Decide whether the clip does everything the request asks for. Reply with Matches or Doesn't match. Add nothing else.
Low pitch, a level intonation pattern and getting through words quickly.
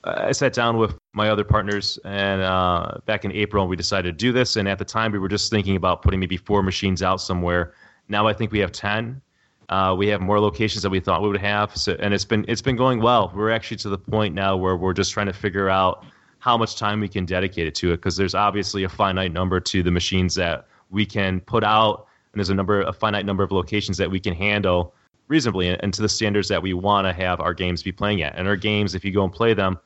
Matches